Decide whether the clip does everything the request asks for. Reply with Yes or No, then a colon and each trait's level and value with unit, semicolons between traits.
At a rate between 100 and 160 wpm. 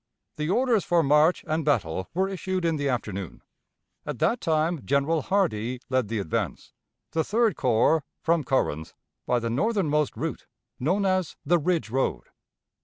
Yes: average, 155 wpm